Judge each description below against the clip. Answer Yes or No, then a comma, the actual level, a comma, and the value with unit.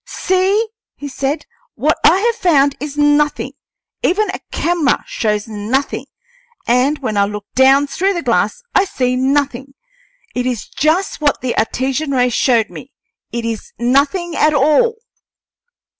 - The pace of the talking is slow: No, average, 145 wpm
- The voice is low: No, very high, 280 Hz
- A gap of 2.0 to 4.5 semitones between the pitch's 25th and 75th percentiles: No, average, 4.9 semitones